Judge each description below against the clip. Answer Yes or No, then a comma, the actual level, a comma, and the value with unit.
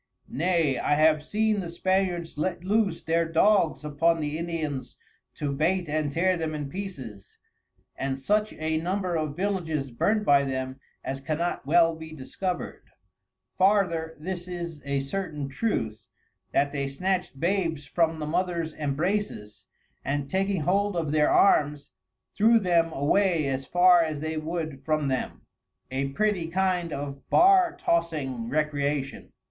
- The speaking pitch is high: No, medium, 160 Hz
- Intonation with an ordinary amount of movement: Yes, average, 4.2 semitones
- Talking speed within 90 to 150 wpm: Yes, average, 145 wpm